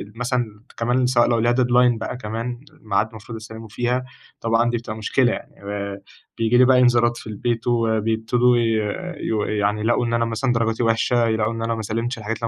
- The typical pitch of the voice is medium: No, low, 115 Hz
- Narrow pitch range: Yes, narrow, 1.6 semitones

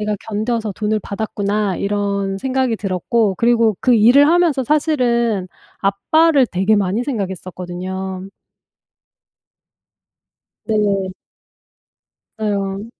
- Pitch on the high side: Yes, high, 210 Hz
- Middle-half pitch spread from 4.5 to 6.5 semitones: No, average, 3.5 semitones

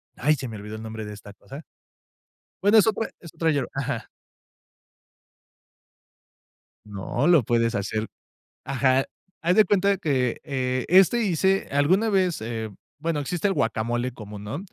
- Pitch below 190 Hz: Yes, low, 135 Hz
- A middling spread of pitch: No, wide, 7.7 semitones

